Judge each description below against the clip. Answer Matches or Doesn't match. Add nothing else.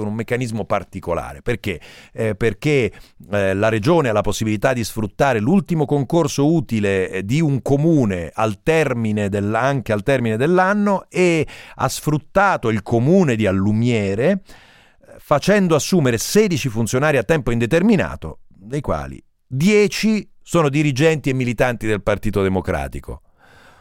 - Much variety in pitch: Matches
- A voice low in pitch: Matches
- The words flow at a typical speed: Matches